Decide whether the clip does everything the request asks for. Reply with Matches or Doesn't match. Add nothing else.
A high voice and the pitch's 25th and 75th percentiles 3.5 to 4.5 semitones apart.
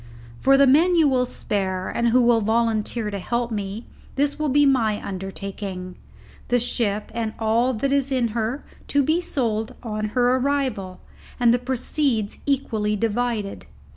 Matches